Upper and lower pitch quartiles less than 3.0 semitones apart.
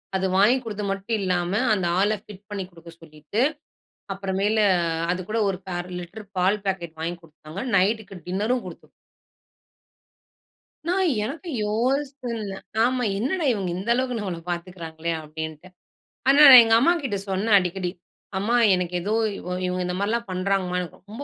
No: average, 4.1 semitones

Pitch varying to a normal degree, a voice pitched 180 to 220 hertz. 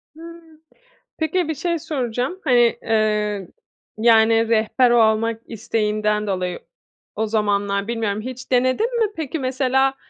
No: average, 4.0 semitones; high, 230 Hz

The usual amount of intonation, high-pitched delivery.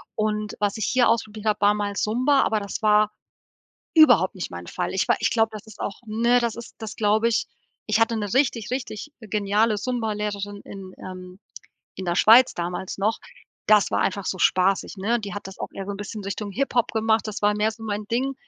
No: narrow, 2.1 semitones; high, 210 Hz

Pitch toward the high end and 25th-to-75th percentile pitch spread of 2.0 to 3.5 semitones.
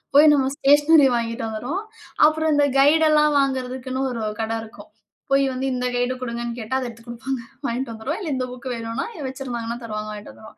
Yes: very high, 255 Hz; average, 3.1 semitones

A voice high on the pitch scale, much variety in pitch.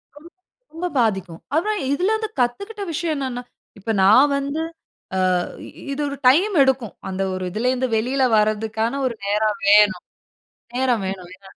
Yes: very high, 250 Hz; wide, 5.7 semitones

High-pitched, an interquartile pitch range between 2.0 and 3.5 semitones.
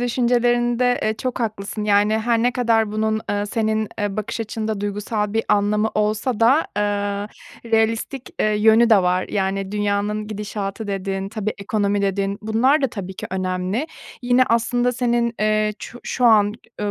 Yes: high, 215 Hz; narrow, 2.4 semitones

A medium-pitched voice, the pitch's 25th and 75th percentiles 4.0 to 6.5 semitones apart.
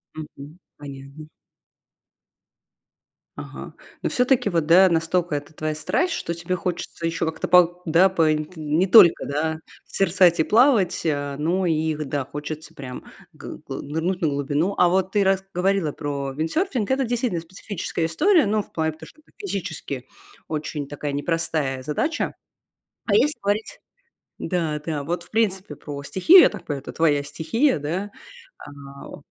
Yes: medium, 165 Hz; average, 4.3 semitones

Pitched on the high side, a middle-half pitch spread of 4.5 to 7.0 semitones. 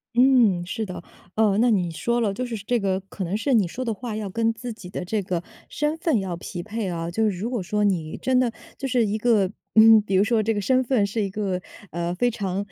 No: high, 210 Hz; average, 4.0 semitones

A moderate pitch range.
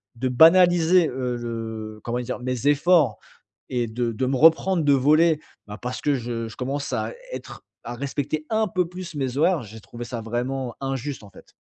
Yes: average, 4.6 semitones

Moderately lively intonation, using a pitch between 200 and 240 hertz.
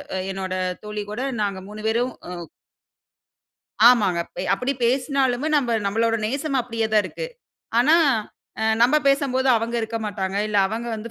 Yes: average, 3.4 semitones; high, 230 Hz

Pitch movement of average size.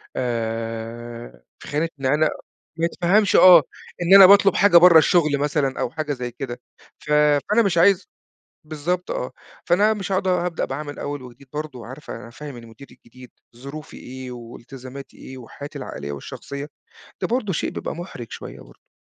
No: wide, 5.7 semitones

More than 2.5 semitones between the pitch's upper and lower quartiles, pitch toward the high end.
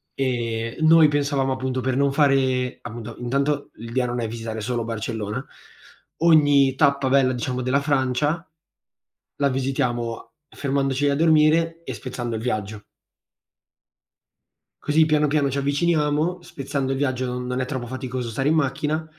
No: average, 2.9 semitones; low, 135 Hz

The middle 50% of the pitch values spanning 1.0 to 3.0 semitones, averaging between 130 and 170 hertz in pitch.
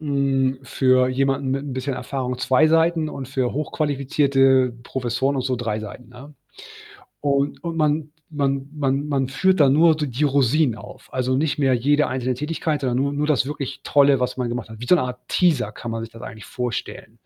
Yes: narrow, 2.5 semitones; low, 135 Hz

